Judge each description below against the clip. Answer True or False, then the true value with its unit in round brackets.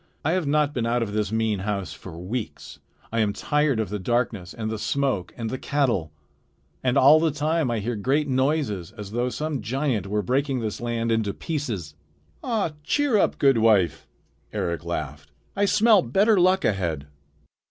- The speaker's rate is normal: True (180 wpm)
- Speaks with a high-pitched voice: False (120 Hz)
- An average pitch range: False (6.2 semitones)